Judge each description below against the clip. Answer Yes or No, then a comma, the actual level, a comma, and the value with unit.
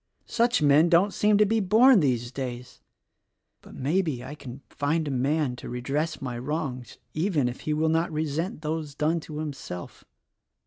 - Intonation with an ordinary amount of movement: Yes, average, 4.1 semitones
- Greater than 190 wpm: No, average, 170 wpm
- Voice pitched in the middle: Yes, medium, 150 Hz